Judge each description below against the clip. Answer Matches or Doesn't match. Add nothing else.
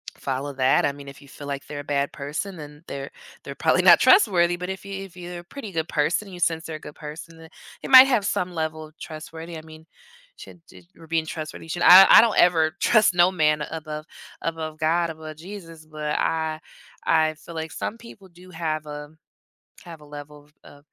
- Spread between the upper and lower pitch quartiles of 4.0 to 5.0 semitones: Doesn't match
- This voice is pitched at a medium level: Matches